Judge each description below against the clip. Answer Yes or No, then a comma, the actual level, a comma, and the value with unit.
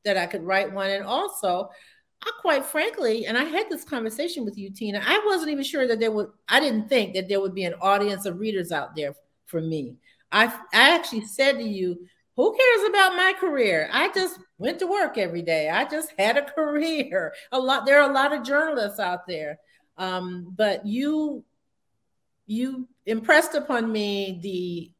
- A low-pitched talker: No, high, 225 Hz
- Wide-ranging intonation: Yes, wide, 7.6 semitones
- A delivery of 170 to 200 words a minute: Yes, average, 195 wpm